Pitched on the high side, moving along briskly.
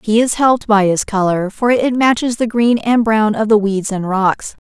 Yes: high, 215 Hz; fast, 230 wpm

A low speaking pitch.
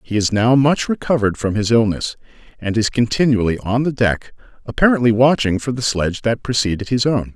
Yes: low, 115 Hz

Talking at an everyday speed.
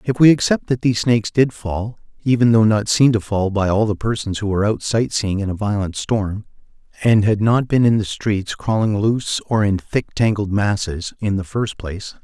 No: fast, 220 wpm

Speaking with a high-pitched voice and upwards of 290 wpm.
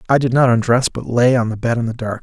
No: low, 120 Hz; fast, 325 wpm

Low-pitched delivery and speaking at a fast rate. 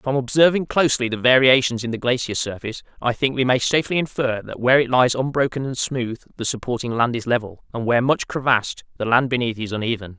Yes: low, 125 Hz; fast, 210 wpm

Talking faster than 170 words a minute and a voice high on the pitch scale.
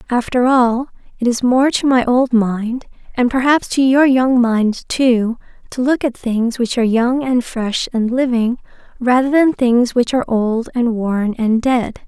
Yes: average, 185 wpm; high, 245 Hz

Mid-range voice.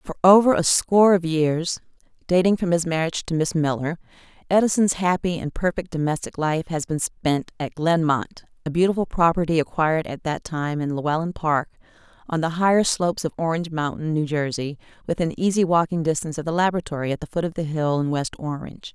Yes: medium, 165 Hz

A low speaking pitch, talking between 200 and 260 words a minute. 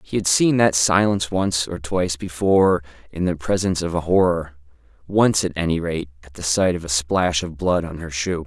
Yes: very low, 85 Hz; fast, 205 wpm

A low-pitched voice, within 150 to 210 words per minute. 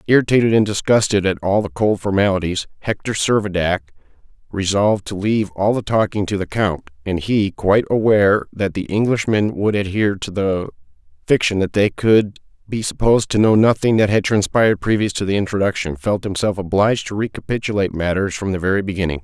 Yes: low, 100 Hz; average, 175 wpm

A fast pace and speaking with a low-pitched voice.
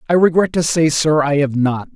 No: fast, 245 wpm; medium, 155 Hz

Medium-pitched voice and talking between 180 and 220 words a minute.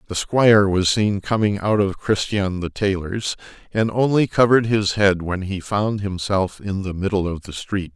No: low, 100 Hz; average, 190 wpm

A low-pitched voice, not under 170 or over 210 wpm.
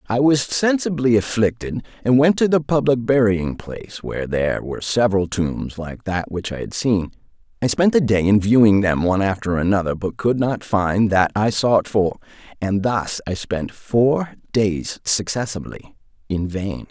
Yes: low, 110 Hz; average, 175 wpm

